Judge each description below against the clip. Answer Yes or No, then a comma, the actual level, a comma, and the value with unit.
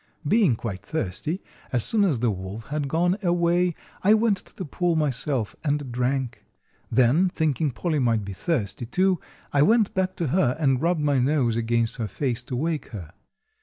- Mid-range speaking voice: Yes, medium, 145 Hz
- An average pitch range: No, wide, 6.6 semitones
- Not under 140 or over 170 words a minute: No, average, 180 wpm